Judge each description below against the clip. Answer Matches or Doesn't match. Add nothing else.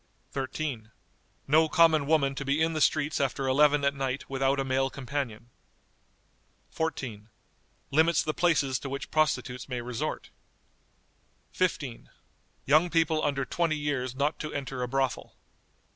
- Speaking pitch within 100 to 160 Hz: Matches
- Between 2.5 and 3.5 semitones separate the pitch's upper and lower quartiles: Matches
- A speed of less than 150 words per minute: Matches